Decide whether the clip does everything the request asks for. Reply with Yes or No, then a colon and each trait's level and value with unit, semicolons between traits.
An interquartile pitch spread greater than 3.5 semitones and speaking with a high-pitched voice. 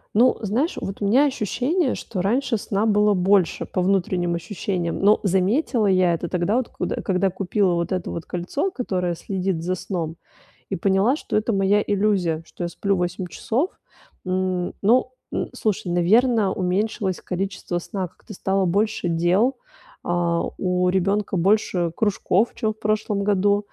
No: average, 2.9 semitones; high, 195 Hz